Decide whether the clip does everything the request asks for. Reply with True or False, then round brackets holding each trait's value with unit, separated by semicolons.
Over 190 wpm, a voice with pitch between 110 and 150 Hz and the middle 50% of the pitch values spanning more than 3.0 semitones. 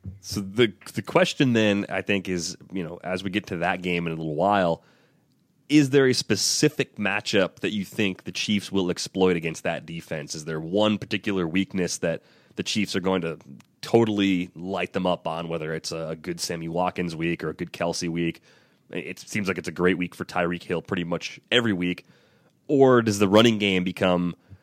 False (200 wpm; 95 Hz; 3.5 semitones)